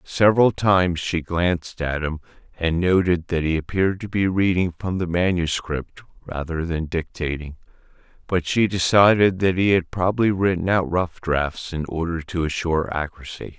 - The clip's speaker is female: No, male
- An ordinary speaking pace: Yes, average, 160 wpm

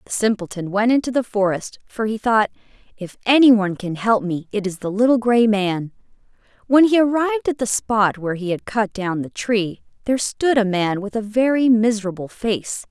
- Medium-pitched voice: No, high, 220 Hz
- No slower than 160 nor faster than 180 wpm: No, average, 195 wpm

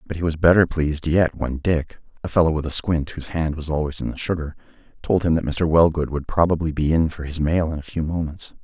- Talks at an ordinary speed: No, fast, 235 wpm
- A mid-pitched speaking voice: No, very low, 80 Hz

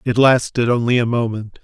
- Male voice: Yes, male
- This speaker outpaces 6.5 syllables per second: No, 5.2 syllables/s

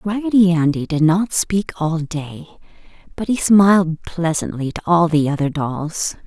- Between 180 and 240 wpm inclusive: No, average, 155 wpm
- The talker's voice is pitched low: No, medium, 170 Hz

